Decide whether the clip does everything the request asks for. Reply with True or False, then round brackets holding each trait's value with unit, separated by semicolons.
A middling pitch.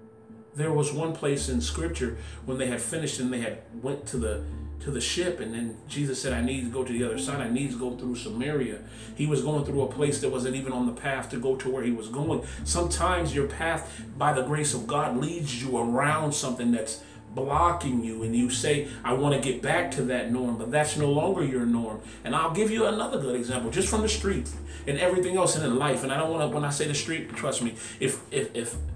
False (125 Hz)